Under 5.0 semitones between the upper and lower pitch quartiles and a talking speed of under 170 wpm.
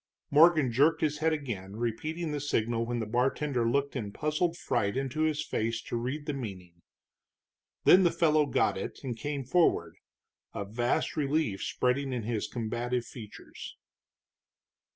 Yes: average, 4.6 semitones; average, 150 wpm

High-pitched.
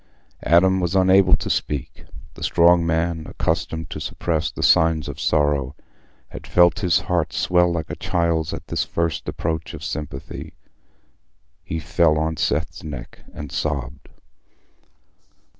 No: very low, 80 Hz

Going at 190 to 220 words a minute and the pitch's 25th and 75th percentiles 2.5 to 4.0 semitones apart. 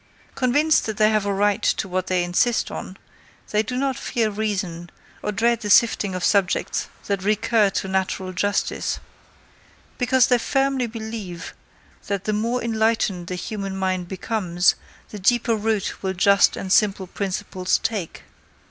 No: average, 155 wpm; average, 3.2 semitones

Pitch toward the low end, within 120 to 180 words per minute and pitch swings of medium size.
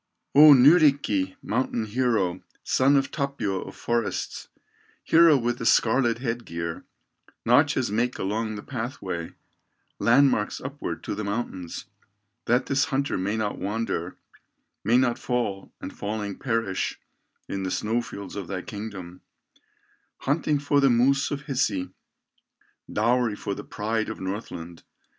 Yes: low, 115 Hz; slow, 135 wpm; average, 4.5 semitones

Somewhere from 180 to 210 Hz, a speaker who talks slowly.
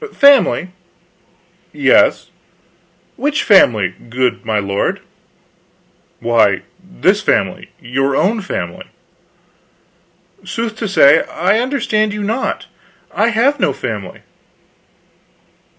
Yes: high, 190 Hz; slow, 90 wpm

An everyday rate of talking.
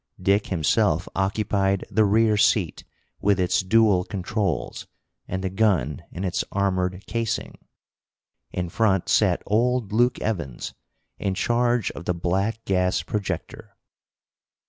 No: slow, 125 wpm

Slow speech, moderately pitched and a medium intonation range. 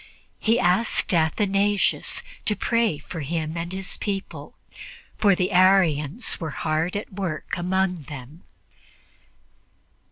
Yes: slow, 115 wpm; medium, 180 Hz; average, 3.8 semitones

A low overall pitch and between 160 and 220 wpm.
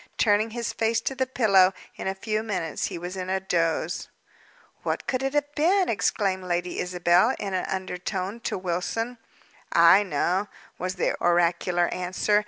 No: high, 190 Hz; average, 165 wpm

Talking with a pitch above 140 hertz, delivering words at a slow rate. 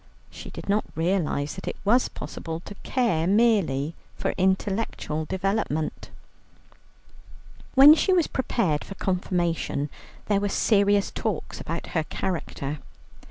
Yes: high, 190 Hz; slow, 120 wpm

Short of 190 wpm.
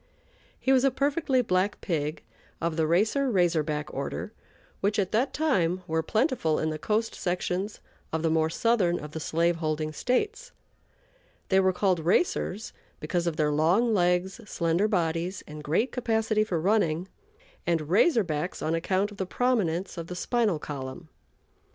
Yes: average, 165 wpm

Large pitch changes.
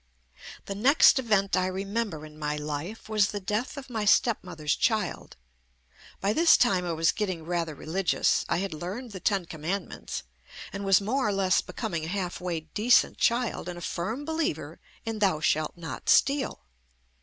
No: average, 4.6 semitones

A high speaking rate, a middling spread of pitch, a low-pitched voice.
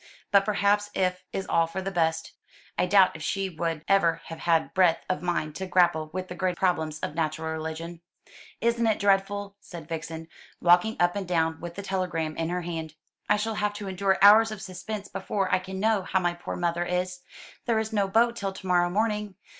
No: fast, 210 wpm; average, 3.1 semitones; medium, 185 Hz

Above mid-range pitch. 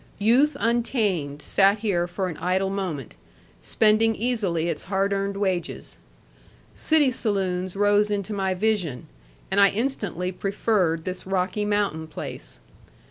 Yes: high, 195 Hz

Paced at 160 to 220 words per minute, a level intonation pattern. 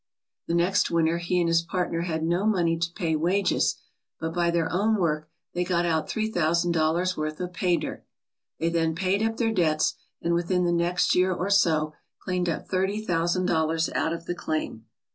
Yes: average, 200 wpm; narrow, 1.9 semitones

